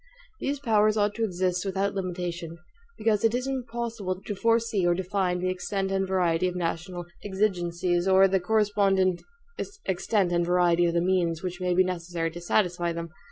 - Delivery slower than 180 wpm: Yes, average, 170 wpm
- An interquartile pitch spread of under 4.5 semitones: Yes, average, 2.7 semitones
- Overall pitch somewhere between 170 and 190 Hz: Yes, medium, 185 Hz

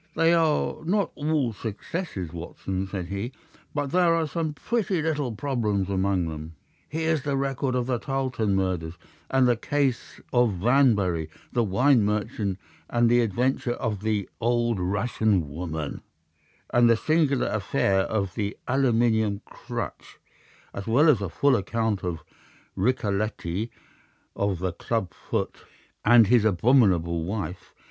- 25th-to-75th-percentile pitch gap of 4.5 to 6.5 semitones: Yes, wide, 5.6 semitones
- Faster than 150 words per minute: No, average, 140 wpm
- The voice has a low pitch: Yes, low, 115 Hz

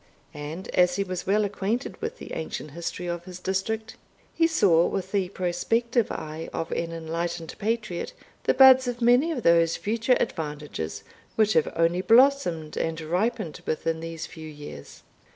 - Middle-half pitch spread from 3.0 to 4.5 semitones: No, wide, 5.5 semitones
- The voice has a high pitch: No, medium, 180 Hz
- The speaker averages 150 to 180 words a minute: Yes, average, 160 wpm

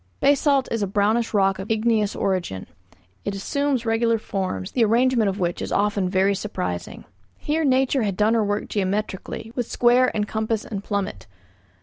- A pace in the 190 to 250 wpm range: No, average, 165 wpm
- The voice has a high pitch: Yes, high, 210 Hz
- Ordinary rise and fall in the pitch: Yes, average, 3.2 semitones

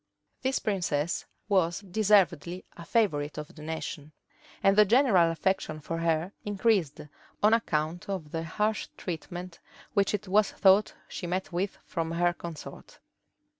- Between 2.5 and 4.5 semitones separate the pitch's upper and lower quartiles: Yes, average, 3.7 semitones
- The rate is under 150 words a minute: Yes, average, 140 wpm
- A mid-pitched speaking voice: Yes, medium, 175 Hz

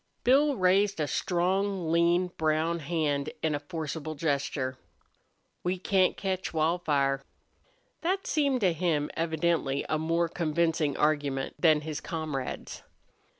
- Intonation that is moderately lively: Yes, average, 3.3 semitones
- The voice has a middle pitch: Yes, medium, 165 Hz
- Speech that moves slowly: Yes, slow, 120 wpm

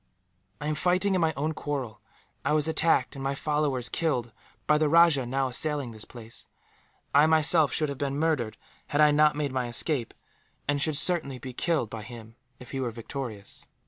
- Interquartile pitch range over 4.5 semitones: No, average, 3.7 semitones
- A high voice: No, medium, 145 Hz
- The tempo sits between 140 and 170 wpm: No, average, 190 wpm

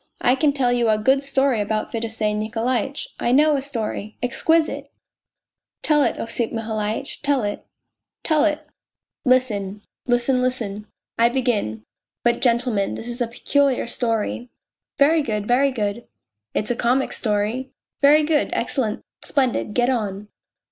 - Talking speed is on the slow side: No, average, 170 wpm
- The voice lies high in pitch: Yes, high, 240 Hz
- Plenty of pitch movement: No, average, 3.8 semitones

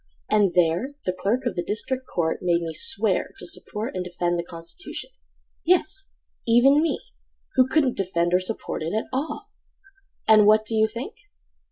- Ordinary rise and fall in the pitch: No, wide, 5.9 semitones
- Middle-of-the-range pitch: No, high, 205 Hz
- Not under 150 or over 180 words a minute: Yes, average, 165 wpm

